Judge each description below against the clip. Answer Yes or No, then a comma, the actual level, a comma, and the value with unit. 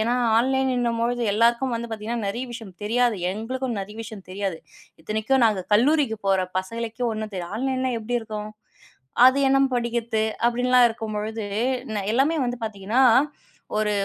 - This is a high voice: Yes, high, 230 Hz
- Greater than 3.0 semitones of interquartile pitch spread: No, narrow, 2.6 semitones